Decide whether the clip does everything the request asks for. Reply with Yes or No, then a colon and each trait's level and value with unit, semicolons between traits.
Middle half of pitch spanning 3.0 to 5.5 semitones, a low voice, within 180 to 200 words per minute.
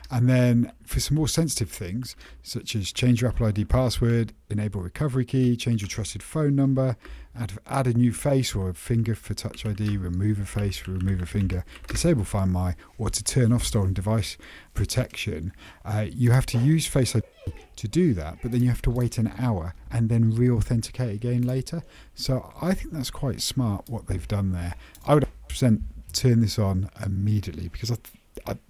Yes: average, 3.9 semitones; low, 115 Hz; average, 195 wpm